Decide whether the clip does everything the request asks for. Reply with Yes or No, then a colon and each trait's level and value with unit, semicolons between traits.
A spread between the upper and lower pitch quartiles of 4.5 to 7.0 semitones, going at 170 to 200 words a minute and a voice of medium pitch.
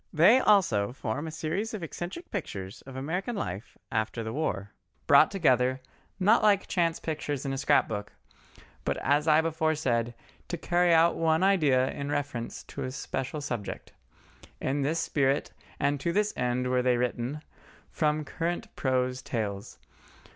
No: average, 4.8 semitones; average, 160 wpm; medium, 145 Hz